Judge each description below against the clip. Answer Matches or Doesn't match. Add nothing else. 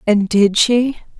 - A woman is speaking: Matches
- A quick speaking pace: Doesn't match